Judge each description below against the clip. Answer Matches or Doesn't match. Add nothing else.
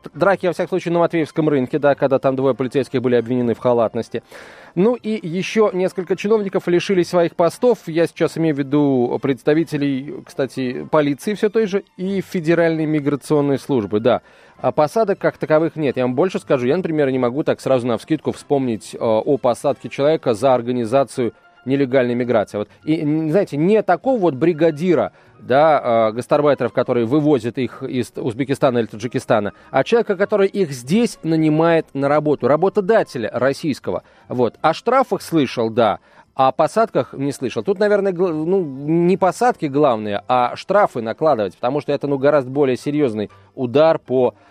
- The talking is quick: Matches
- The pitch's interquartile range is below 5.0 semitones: Doesn't match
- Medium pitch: Matches